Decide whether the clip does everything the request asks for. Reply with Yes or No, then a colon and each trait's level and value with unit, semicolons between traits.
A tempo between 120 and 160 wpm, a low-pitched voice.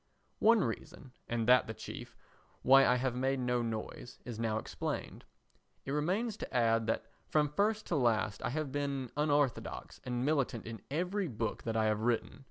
No: average, 180 wpm; low, 125 Hz